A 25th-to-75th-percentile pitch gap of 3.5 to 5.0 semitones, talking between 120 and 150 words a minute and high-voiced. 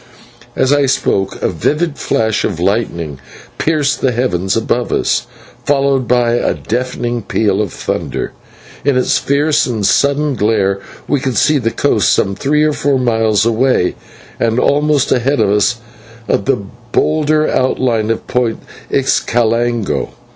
No: average, 4.1 semitones; average, 140 wpm; low, 120 Hz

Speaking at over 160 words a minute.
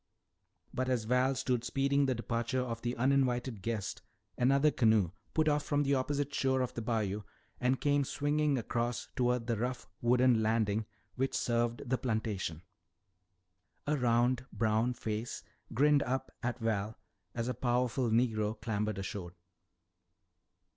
No: average, 140 wpm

